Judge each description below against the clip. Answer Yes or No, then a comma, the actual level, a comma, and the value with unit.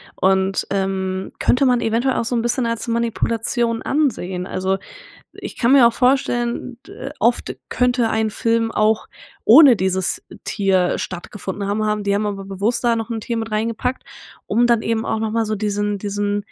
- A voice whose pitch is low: No, high, 220 Hz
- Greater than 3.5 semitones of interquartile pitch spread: No, average, 2.8 semitones